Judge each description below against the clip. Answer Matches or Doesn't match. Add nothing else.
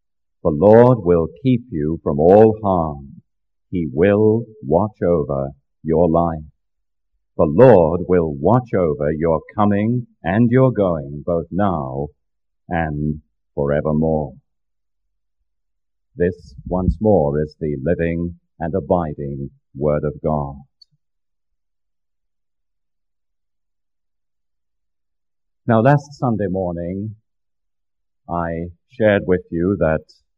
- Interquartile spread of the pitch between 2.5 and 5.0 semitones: Doesn't match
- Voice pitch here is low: Matches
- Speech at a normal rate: Doesn't match